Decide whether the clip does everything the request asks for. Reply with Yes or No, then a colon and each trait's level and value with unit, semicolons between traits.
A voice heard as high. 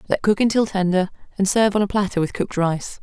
Yes: high, 195 Hz